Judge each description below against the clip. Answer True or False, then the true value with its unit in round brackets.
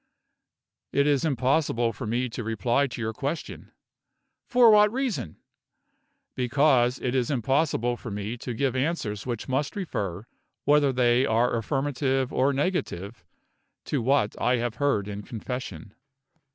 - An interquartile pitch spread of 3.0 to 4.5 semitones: True (3.6 semitones)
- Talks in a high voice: False (125 Hz)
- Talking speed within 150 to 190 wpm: False (140 wpm)